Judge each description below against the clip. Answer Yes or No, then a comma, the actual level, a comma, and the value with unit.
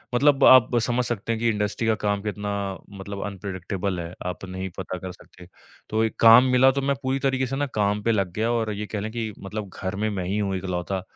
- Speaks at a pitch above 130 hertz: No, low, 105 Hz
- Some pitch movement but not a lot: Yes, average, 3.3 semitones